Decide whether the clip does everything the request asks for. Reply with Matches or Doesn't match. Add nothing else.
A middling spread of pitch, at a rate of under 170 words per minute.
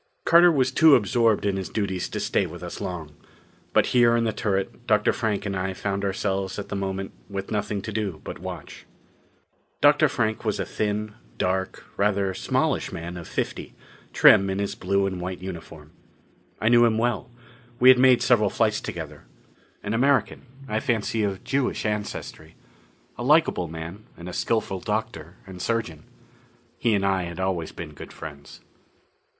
Doesn't match